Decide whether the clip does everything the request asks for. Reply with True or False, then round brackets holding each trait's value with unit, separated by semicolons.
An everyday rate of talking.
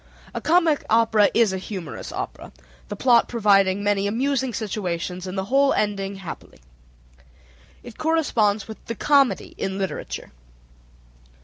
False (130 wpm)